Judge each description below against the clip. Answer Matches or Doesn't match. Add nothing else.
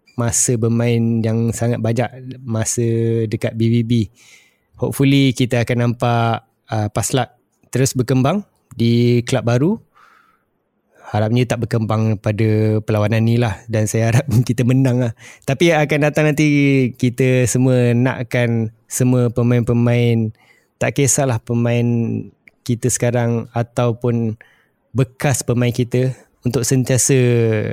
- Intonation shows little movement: Matches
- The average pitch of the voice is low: Matches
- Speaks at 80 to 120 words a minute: Matches